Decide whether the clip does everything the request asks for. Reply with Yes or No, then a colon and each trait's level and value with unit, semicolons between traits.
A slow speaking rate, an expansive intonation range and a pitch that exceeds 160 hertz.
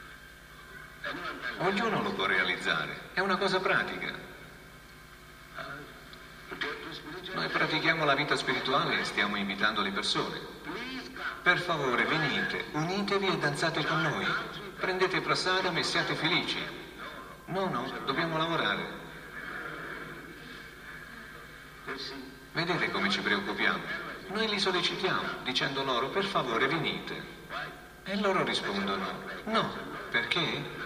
No: slow, 100 wpm; average, 4.1 semitones; medium, 185 Hz